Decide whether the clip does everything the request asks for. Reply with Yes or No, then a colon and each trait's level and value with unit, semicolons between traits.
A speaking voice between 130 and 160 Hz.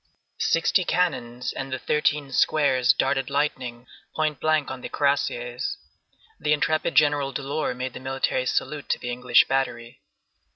Yes: medium, 140 Hz